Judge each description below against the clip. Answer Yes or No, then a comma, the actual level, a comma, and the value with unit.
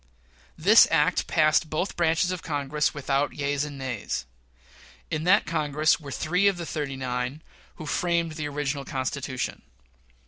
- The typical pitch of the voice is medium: Yes, medium, 150 Hz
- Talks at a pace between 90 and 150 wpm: Yes, average, 145 wpm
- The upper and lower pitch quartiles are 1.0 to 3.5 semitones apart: Yes, average, 2.8 semitones